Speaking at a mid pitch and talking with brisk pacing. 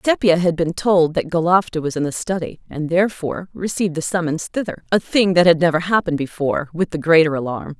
No: medium, 170 Hz; average, 190 wpm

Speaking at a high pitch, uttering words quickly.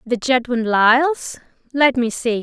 No: very high, 250 Hz; slow, 125 wpm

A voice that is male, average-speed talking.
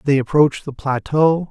Yes: male; average, 160 wpm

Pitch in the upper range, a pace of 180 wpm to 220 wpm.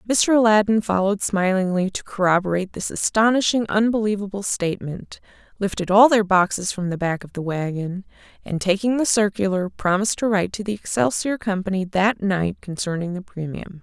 No: high, 195 Hz; average, 155 wpm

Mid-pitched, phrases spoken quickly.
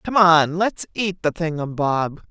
Yes: medium, 170 Hz; fast, 210 wpm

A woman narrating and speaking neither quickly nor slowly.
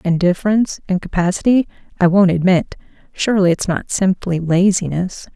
No: female; slow, 100 wpm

